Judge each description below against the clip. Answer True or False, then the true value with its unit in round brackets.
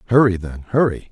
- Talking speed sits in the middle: True (160 wpm)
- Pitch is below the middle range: True (105 Hz)